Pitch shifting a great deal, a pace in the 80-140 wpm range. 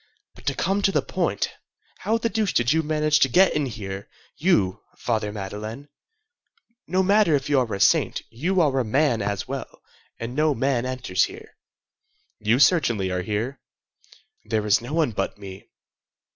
No: wide, 6.6 semitones; average, 170 wpm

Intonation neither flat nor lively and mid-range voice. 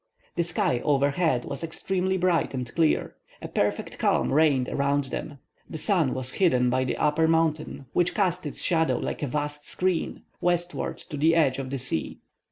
Yes: average, 4.0 semitones; medium, 150 Hz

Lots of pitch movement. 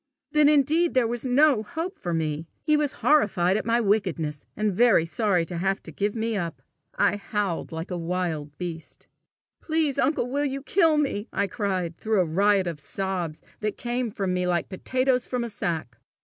Yes: wide, 6.6 semitones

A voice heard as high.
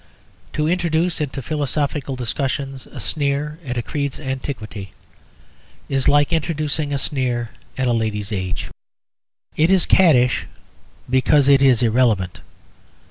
No: low, 135 Hz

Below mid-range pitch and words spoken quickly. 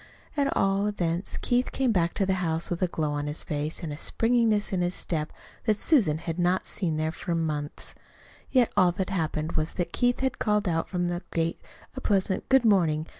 No: medium, 175 Hz; fast, 215 wpm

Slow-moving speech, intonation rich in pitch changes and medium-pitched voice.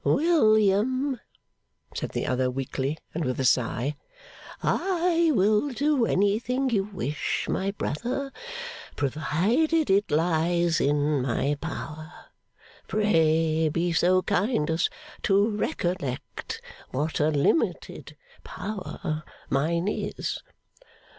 Yes: slow, 100 wpm; wide, 6.3 semitones; medium, 175 Hz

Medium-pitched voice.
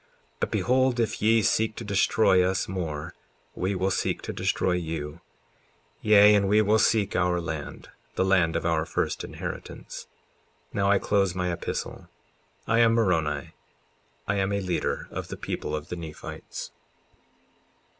No: very low, 95 Hz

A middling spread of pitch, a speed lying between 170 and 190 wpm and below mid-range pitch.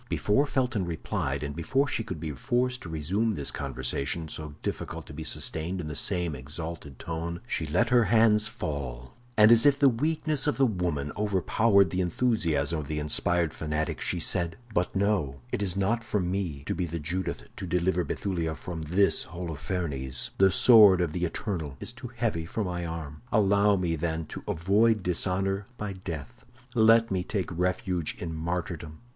Yes: average, 4.8 semitones; average, 180 wpm; very low, 90 Hz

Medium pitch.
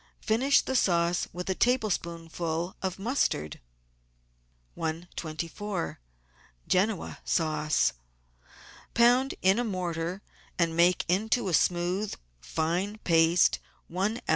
Yes: medium, 175 Hz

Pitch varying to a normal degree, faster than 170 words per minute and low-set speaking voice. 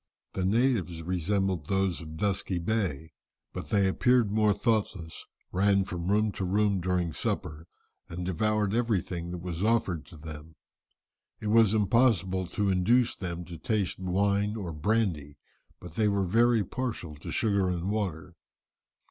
No: average, 3.5 semitones; average, 150 wpm; very low, 95 Hz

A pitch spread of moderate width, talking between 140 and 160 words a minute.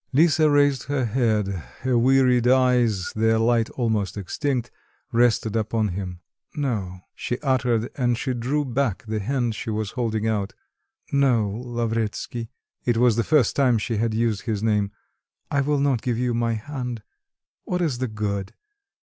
Yes: average, 3.0 semitones; average, 155 wpm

